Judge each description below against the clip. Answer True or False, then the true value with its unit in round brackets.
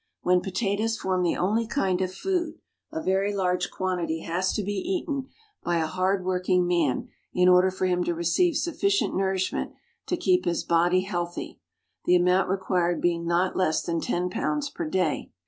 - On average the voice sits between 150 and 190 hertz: True (185 Hz)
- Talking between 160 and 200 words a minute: True (175 wpm)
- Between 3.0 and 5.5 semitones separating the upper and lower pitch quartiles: False (2.4 semitones)